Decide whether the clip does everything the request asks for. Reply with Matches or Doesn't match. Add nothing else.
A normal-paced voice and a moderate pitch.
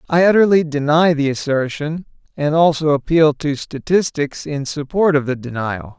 Matches